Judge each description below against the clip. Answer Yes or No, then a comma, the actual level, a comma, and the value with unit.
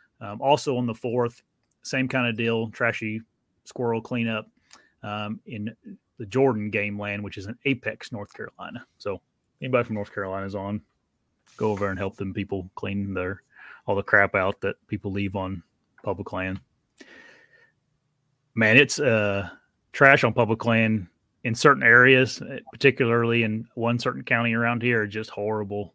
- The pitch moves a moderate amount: Yes, average, 3.2 semitones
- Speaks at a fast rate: No, average, 155 wpm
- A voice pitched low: Yes, low, 110 Hz